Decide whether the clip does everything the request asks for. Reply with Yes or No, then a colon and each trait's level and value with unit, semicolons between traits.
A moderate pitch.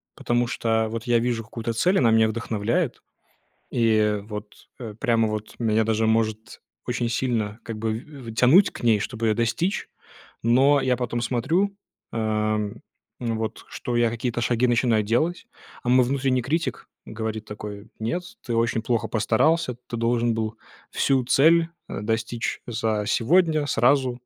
No: low, 115 Hz